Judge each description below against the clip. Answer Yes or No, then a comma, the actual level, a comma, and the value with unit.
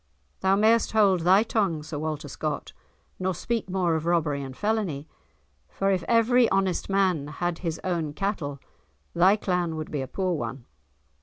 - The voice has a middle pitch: Yes, medium, 180 Hz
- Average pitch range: Yes, average, 4.0 semitones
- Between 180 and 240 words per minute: No, average, 165 wpm